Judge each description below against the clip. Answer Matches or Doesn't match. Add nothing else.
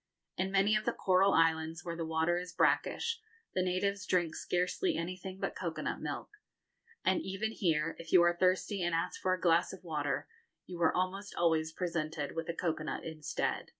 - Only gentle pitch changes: Matches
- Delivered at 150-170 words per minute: Doesn't match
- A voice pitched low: Doesn't match